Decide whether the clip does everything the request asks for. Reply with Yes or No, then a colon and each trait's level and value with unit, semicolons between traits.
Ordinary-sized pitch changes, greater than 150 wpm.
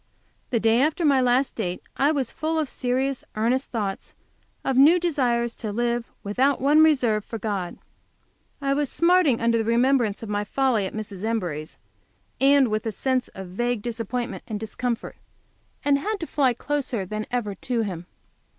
Yes: average, 4.2 semitones; average, 170 wpm